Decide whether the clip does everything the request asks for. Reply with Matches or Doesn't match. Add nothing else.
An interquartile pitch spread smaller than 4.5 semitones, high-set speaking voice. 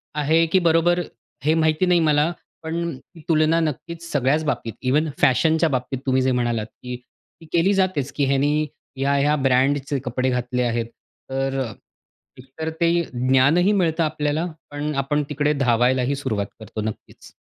Doesn't match